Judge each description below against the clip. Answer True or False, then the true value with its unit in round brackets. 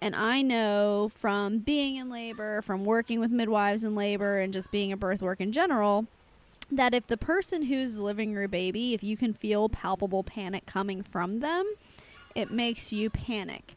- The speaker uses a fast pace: False (185 wpm)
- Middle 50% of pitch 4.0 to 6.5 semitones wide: False (2.8 semitones)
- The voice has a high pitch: True (215 Hz)